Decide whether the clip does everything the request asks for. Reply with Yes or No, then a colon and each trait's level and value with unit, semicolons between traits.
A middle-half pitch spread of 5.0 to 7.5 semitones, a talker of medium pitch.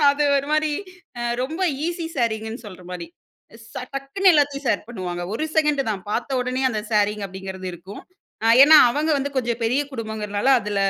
No: wide, 5.4 semitones; high, 240 Hz